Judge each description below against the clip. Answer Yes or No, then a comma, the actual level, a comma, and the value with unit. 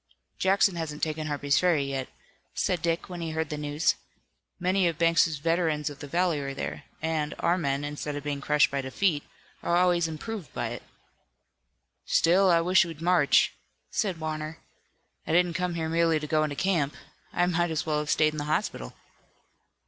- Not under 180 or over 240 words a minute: Yes, average, 185 wpm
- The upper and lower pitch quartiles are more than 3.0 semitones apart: No, average, 2.7 semitones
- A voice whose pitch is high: No, medium, 160 Hz